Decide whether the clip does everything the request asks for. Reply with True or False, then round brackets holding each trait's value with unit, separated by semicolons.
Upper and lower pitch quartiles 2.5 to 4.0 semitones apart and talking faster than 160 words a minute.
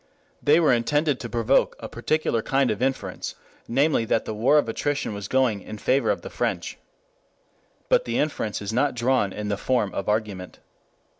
False (4.6 semitones; 180 wpm)